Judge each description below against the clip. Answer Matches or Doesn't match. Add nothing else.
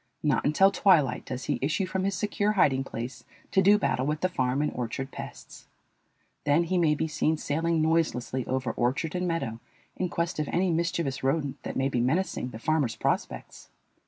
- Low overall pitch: Doesn't match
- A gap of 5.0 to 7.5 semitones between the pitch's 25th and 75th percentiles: Doesn't match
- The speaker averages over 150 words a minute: Matches